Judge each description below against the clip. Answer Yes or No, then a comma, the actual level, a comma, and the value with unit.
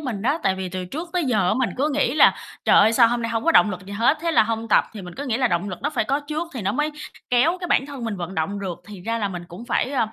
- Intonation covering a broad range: Yes, wide, 6.3 semitones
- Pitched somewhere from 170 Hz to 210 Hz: No, high, 230 Hz